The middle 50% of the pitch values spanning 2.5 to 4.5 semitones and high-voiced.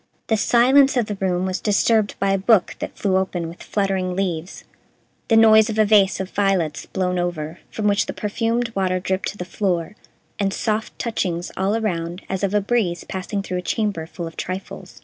Yes: average, 2.9 semitones; high, 195 Hz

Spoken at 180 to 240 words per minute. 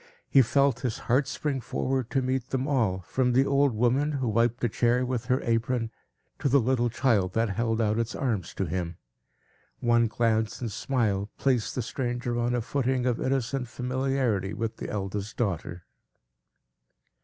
No: average, 170 wpm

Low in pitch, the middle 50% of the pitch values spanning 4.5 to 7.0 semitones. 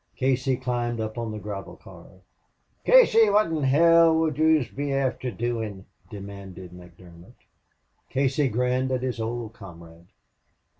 Yes: low, 120 Hz; wide, 5.4 semitones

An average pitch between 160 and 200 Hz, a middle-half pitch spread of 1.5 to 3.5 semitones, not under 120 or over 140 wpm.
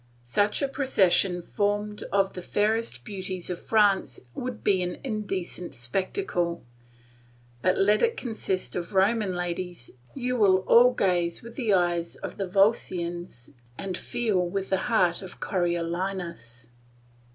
Yes: high, 190 Hz; average, 3.2 semitones; slow, 135 wpm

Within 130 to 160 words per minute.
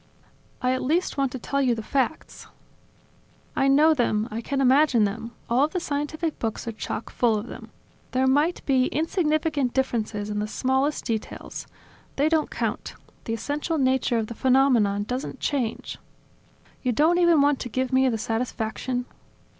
No: average, 170 wpm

